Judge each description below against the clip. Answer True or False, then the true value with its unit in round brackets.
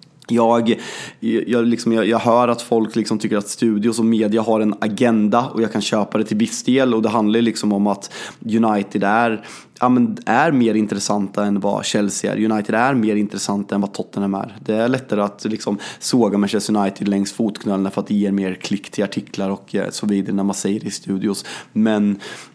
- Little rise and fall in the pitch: True (2.2 semitones)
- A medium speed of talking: False (205 wpm)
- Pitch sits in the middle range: False (110 Hz)